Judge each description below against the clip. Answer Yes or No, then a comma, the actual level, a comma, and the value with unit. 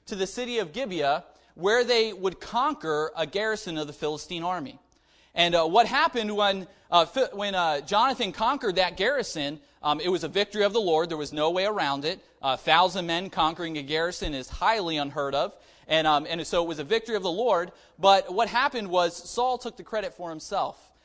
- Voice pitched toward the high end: No, medium, 180 Hz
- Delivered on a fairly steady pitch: No, average, 4.8 semitones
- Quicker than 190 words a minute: Yes, fast, 205 wpm